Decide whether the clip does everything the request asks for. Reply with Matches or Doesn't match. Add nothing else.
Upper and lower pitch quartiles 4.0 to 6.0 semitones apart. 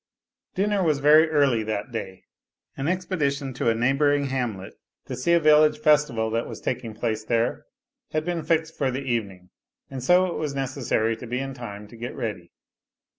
Matches